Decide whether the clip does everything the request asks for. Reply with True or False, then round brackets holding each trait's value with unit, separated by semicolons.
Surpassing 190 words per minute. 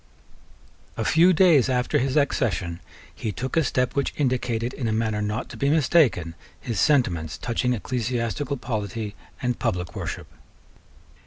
False (145 wpm)